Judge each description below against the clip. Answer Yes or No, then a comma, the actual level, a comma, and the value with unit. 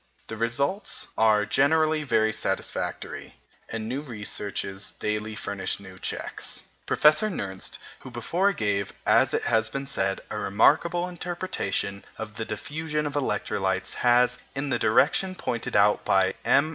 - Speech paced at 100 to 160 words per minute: Yes, slow, 135 wpm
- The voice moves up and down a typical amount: No, wide, 6.6 semitones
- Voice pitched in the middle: No, low, 115 Hz